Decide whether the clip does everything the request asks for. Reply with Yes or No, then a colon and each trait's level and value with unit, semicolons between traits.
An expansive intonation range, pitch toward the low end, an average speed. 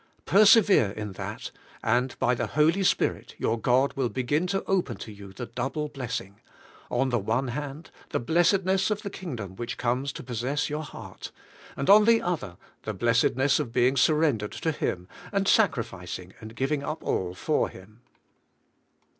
Yes: wide, 6.0 semitones; low, 130 Hz; average, 170 wpm